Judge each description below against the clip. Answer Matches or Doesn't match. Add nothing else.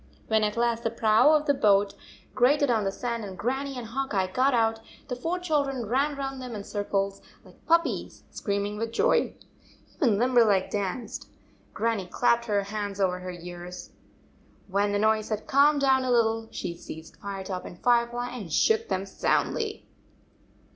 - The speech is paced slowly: Doesn't match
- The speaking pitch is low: Doesn't match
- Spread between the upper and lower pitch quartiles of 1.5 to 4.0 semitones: Doesn't match